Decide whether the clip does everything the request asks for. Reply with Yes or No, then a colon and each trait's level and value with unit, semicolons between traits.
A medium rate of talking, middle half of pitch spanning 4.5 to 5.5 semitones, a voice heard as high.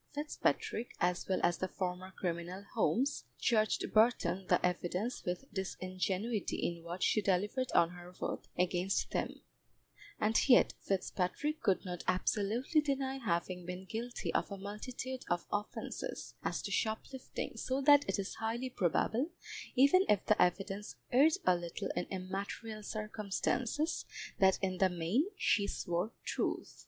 Yes: average, 145 wpm; average, 4.9 semitones; high, 200 Hz